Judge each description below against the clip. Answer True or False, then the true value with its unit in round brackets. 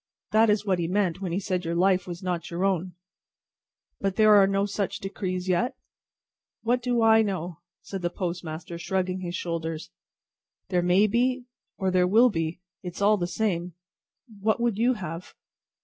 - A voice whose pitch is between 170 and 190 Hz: True (185 Hz)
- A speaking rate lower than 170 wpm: False (180 wpm)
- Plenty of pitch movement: False (3.2 semitones)